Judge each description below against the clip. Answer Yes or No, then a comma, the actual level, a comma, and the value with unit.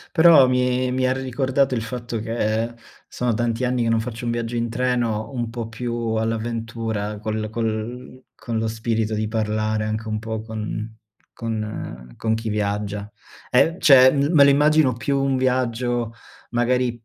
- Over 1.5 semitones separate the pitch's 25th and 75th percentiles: Yes, narrow, 2.4 semitones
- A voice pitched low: Yes, low, 115 Hz